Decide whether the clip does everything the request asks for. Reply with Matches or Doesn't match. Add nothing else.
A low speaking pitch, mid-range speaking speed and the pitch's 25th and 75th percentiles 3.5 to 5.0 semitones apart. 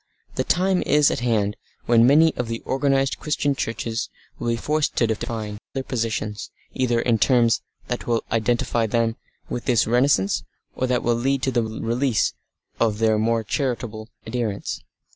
Doesn't match